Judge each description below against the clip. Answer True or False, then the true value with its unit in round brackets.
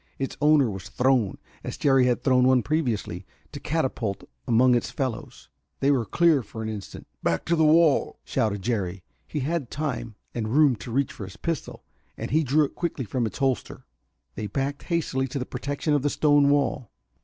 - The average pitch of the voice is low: True (130 Hz)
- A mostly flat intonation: False (4.3 semitones)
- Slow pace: False (190 wpm)